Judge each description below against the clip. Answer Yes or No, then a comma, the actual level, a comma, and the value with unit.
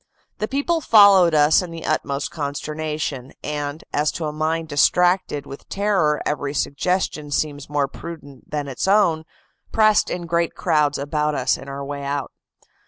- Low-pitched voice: No, medium, 150 Hz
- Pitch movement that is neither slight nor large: Yes, average, 3.1 semitones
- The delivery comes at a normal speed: Yes, average, 160 wpm